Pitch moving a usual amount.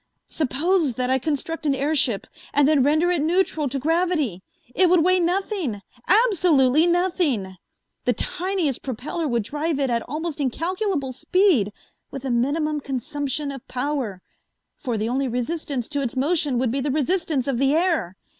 Yes: average, 4.7 semitones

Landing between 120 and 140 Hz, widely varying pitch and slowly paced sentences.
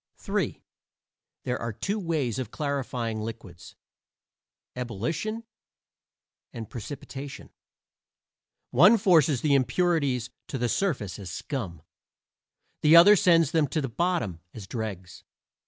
Yes: low, 135 Hz; wide, 6.7 semitones; slow, 110 wpm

